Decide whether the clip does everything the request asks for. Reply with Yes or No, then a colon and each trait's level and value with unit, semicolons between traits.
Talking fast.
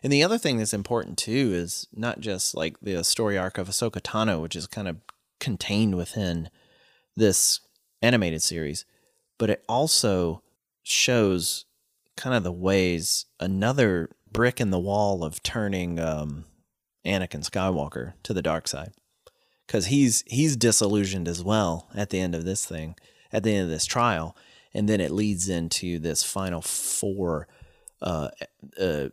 No: average, 155 wpm